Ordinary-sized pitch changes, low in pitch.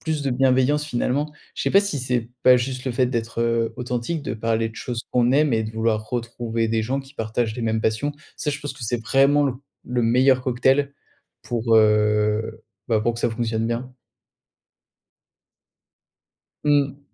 Yes: average, 3.1 semitones; low, 120 Hz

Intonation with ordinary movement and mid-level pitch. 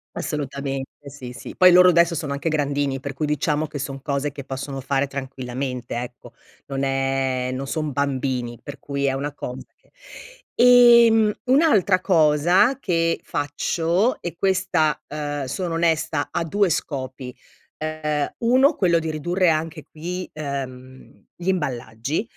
Yes: average, 4.2 semitones; medium, 145 Hz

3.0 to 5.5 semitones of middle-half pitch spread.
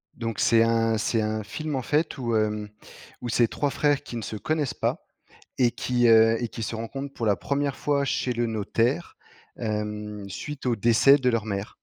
Yes: average, 3.8 semitones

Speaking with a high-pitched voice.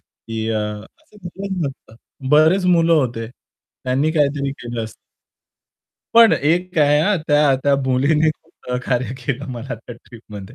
No: medium, 140 Hz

